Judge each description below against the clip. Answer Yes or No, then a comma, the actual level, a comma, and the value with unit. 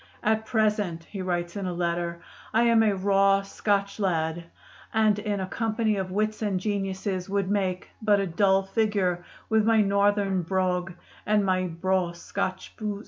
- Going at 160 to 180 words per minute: Yes, average, 165 wpm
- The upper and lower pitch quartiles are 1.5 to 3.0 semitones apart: Yes, narrow, 2.4 semitones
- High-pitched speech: Yes, high, 195 Hz